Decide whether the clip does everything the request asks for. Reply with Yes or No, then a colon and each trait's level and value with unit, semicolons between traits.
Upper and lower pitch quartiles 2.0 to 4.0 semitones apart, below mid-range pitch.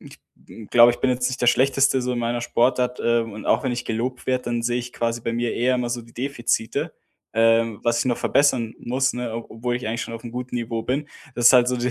No: narrow, 1.3 semitones; low, 120 Hz